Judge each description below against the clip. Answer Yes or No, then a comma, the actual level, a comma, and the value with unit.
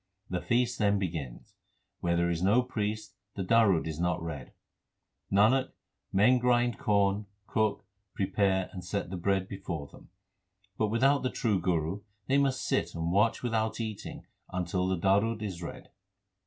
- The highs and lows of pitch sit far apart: No, average, 4.1 semitones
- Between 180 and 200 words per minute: No, average, 155 wpm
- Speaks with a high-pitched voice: No, low, 100 Hz